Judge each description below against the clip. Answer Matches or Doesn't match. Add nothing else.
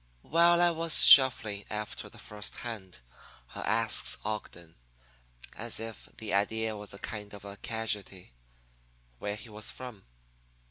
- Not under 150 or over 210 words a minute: Doesn't match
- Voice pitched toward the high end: Doesn't match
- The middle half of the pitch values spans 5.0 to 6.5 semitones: Doesn't match